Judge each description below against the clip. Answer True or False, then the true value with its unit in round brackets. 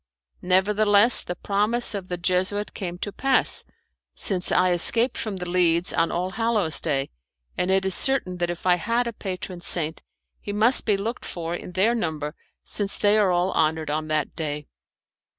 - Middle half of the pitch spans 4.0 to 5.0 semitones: False (3.3 semitones)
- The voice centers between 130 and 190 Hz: True (185 Hz)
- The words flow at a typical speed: True (180 wpm)